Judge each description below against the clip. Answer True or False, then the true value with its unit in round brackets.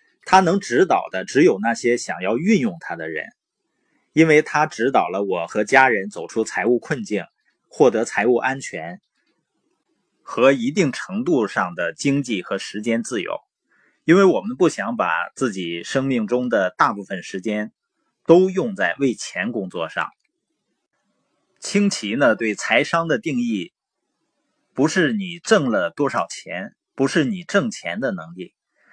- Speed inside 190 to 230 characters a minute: True (215 characters per minute)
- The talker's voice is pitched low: False (150 Hz)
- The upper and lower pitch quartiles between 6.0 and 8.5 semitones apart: False (9.0 semitones)